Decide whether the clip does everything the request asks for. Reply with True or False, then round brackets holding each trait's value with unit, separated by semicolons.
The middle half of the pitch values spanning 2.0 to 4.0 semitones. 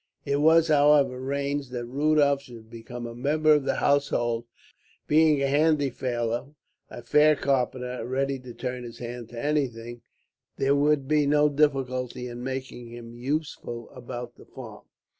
True (3.2 semitones)